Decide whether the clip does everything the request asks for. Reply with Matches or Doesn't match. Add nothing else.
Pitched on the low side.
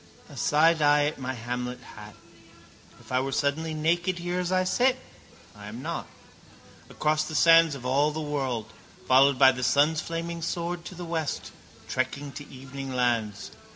Doesn't match